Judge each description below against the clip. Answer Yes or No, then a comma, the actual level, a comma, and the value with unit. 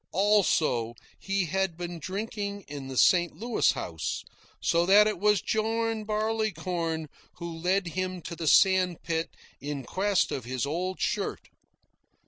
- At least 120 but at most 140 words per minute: Yes, slow, 135 wpm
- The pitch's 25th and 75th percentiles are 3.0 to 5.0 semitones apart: Yes, average, 4.0 semitones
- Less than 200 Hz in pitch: Yes, medium, 185 Hz